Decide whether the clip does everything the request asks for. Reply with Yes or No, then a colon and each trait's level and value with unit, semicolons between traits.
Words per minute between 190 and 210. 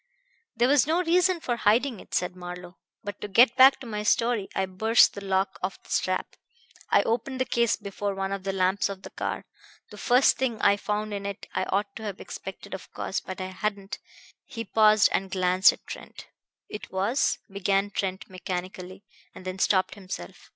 Yes: average, 200 wpm